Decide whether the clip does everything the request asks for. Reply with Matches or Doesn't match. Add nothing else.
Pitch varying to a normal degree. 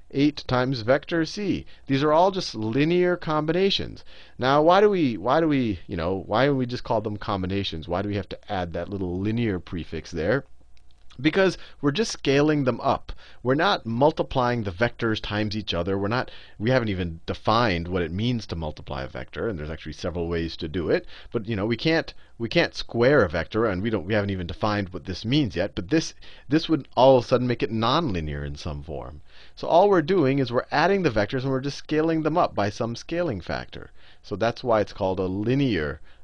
Doesn't match